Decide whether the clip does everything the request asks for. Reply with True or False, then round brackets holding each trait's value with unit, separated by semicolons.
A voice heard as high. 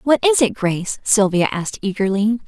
True (210 Hz)